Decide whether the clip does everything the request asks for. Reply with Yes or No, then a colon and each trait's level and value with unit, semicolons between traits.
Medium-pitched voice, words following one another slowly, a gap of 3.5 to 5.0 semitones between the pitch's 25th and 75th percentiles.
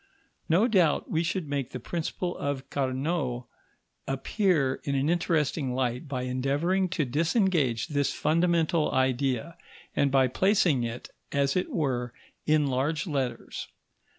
Yes: medium, 145 Hz; slow, 130 wpm; average, 4.4 semitones